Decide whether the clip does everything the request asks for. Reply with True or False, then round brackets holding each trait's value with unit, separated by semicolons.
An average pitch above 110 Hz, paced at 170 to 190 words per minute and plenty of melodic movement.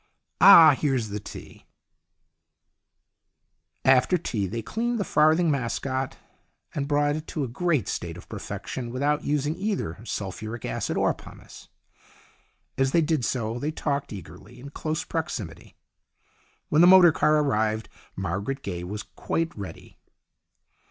False (135 Hz; 140 wpm; 6.1 semitones)